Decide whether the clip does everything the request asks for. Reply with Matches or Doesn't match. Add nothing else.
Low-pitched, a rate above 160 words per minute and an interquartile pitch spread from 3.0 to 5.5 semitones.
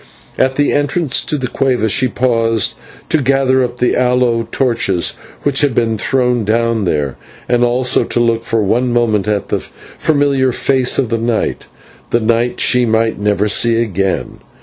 Doesn't match